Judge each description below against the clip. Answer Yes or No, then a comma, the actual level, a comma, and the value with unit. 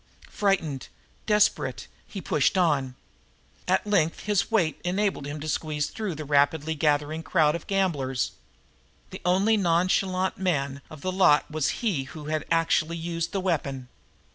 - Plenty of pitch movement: No, average, 4.2 semitones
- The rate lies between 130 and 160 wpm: Yes, average, 145 wpm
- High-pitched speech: No, medium, 165 Hz